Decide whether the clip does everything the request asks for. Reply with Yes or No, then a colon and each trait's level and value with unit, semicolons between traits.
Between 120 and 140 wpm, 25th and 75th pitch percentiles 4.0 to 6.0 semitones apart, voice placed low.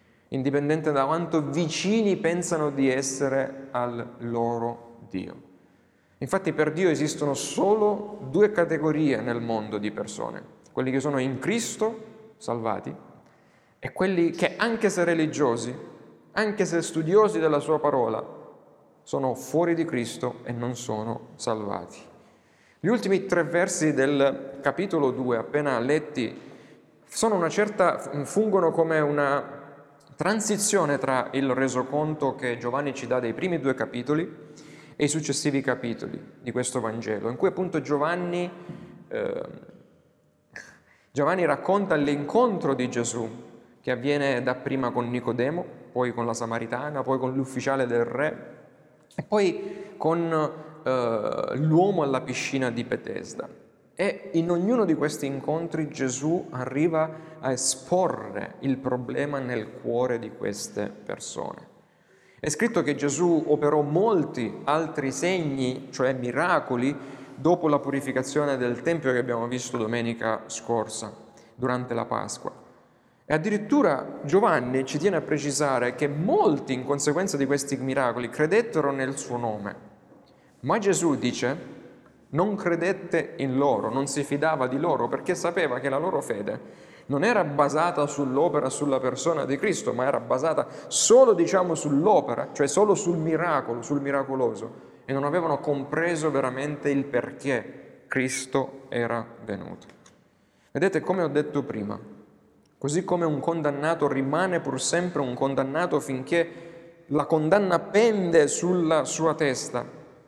No: average, 130 wpm; average, 4.7 semitones; medium, 145 Hz